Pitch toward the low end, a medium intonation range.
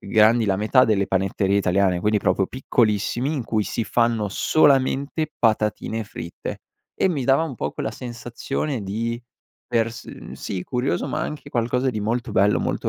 Yes: low, 115 Hz; average, 3.7 semitones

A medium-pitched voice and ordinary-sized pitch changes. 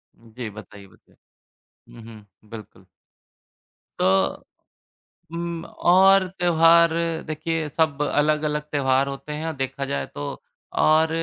Yes: medium, 150 Hz; average, 4.5 semitones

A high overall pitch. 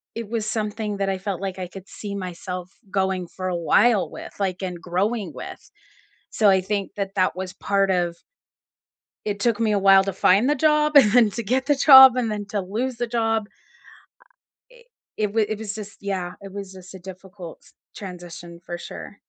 Yes: high, 200 Hz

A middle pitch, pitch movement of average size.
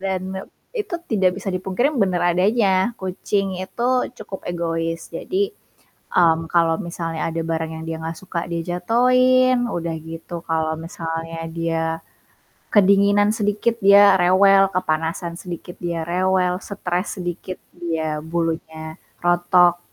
Yes: medium, 180 Hz; average, 3.0 semitones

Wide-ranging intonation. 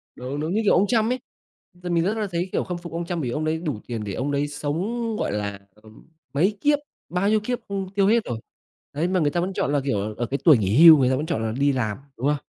Yes: wide, 6.8 semitones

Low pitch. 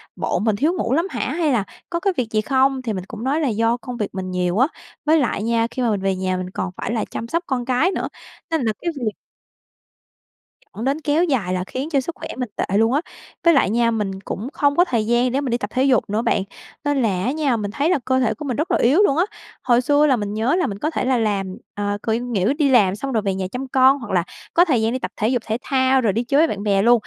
No: high, 245 Hz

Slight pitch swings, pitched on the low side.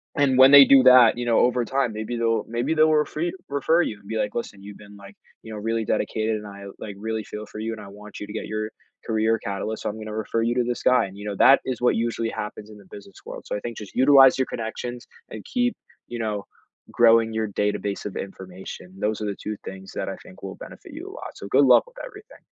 No: average, 3.0 semitones; low, 110 Hz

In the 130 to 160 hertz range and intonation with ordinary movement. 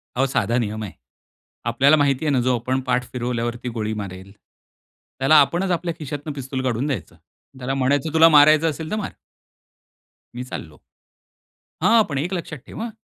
Yes: low, 135 Hz; average, 4.0 semitones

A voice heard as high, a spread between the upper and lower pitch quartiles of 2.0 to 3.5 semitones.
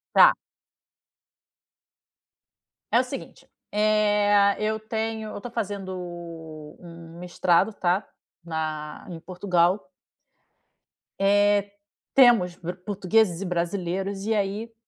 Yes: high, 200 Hz; average, 3.2 semitones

